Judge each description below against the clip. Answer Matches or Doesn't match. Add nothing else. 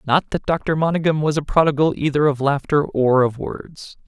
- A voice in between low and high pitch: Matches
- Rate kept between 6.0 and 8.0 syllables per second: Doesn't match